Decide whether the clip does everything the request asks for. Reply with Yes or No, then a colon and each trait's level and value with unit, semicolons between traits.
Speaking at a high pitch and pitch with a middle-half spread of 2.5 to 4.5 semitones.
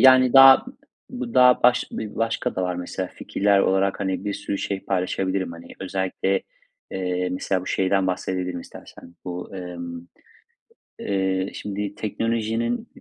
No: very low, 95 Hz; average, 2.8 semitones